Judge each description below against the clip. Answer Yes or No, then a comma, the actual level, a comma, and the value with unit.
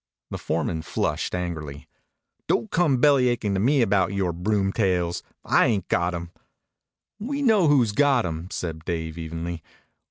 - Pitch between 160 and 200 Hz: No, very low, 95 Hz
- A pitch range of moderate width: No, wide, 6.5 semitones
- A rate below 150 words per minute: Yes, average, 140 wpm